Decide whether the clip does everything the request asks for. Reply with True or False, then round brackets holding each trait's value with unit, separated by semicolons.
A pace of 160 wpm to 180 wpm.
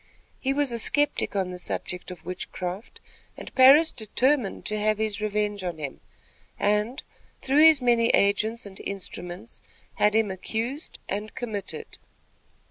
False (140 wpm)